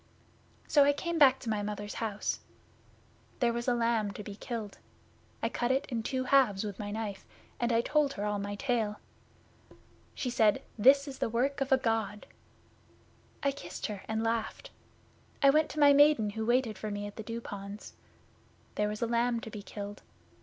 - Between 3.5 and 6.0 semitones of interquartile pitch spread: Yes, average, 4.0 semitones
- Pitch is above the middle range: Yes, high, 230 Hz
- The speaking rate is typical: Yes, average, 190 wpm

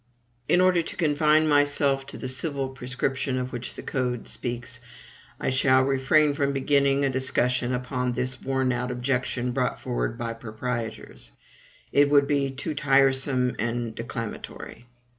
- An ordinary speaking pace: Yes, average, 145 wpm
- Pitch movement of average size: No, narrow, 2.0 semitones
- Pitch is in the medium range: No, low, 130 Hz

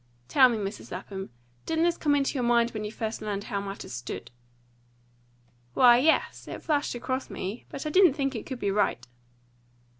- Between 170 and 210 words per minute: Yes, average, 185 wpm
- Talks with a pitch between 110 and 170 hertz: No, high, 235 Hz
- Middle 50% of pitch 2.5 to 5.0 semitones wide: No, wide, 5.4 semitones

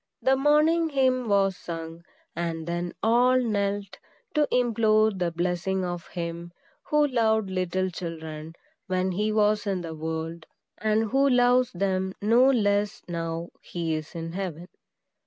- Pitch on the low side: No, high, 195 Hz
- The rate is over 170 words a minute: No, average, 140 wpm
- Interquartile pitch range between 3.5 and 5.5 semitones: Yes, average, 5.1 semitones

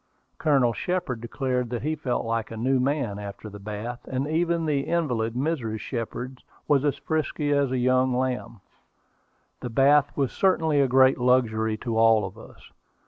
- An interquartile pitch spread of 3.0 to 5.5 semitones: Yes, average, 3.9 semitones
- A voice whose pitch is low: Yes, low, 130 Hz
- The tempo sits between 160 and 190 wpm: Yes, average, 170 wpm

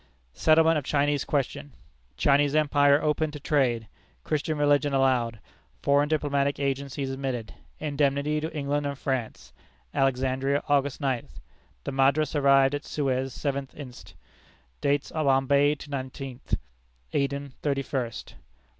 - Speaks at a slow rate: Yes, slow, 125 wpm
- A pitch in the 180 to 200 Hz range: No, medium, 140 Hz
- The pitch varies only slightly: Yes, narrow, 1.5 semitones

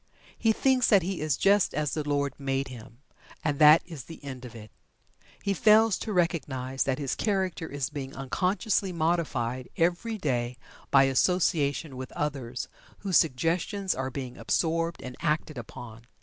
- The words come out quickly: No, average, 160 wpm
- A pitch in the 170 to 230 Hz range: No, medium, 150 Hz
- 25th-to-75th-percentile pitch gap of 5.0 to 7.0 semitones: Yes, wide, 5.4 semitones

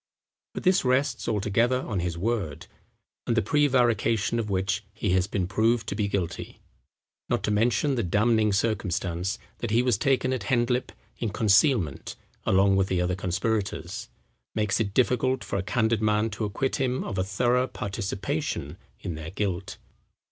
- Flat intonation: No, average, 4.0 semitones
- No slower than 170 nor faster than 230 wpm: No, average, 160 wpm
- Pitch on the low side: Yes, low, 105 Hz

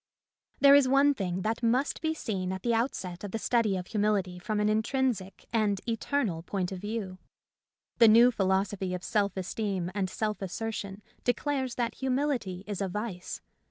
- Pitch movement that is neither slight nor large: Yes, average, 4.0 semitones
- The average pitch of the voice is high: Yes, high, 210 Hz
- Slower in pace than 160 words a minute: No, average, 170 wpm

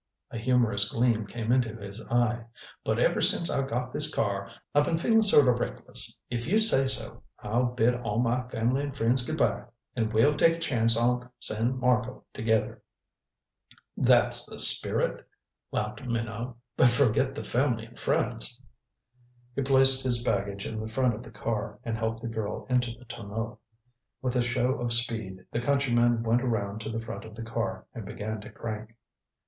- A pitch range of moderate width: No, narrow, 2.3 semitones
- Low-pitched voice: Yes, low, 120 Hz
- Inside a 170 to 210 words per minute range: Yes, average, 180 wpm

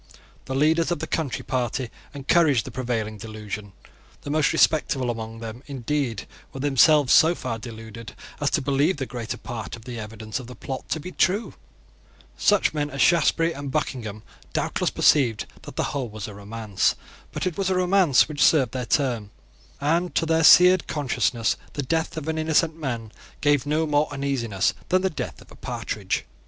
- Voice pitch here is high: No, low, 135 Hz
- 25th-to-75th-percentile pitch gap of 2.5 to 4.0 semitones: No, wide, 5.5 semitones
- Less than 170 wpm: No, average, 180 wpm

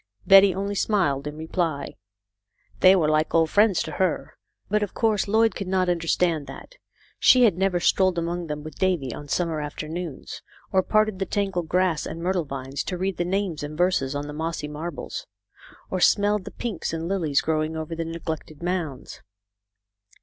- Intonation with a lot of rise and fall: No, average, 3.6 semitones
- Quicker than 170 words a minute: Yes, average, 180 wpm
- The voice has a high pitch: No, medium, 175 Hz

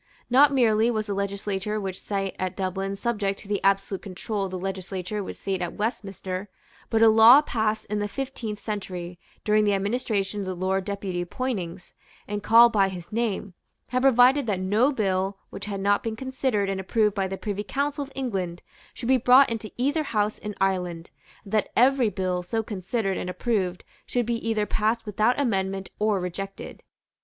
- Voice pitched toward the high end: Yes, high, 205 Hz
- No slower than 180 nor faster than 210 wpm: Yes, average, 185 wpm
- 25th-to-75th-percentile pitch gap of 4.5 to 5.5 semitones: No, average, 3.0 semitones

